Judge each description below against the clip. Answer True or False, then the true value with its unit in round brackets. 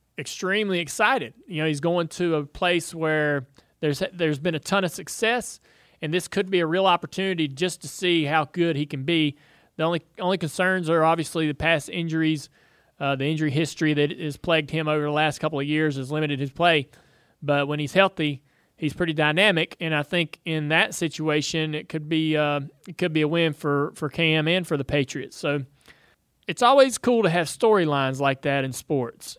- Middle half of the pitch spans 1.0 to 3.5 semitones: True (2.9 semitones)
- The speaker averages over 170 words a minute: True (200 wpm)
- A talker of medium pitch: True (160 Hz)